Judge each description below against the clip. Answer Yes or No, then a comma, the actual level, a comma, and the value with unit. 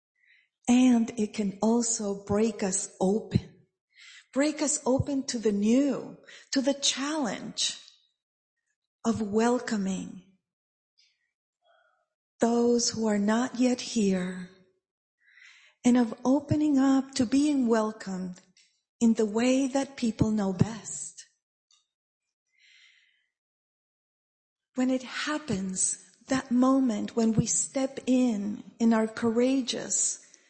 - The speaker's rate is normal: No, slow, 100 wpm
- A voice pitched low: No, high, 235 Hz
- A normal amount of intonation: Yes, average, 4.1 semitones